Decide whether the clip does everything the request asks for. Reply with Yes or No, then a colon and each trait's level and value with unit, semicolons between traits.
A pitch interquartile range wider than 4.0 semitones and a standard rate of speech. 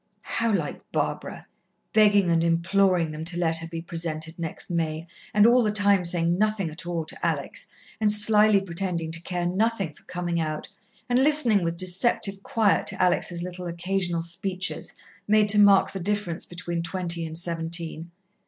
No: average, 3.4 semitones; average, 170 wpm